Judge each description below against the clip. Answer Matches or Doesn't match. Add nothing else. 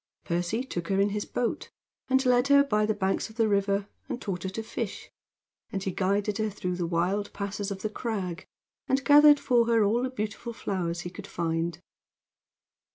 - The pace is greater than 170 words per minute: Matches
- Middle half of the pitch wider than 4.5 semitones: Doesn't match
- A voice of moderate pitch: Doesn't match